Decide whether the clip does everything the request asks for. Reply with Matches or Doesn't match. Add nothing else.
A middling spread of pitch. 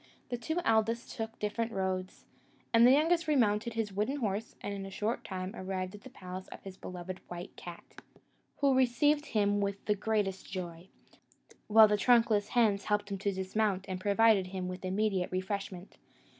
Matches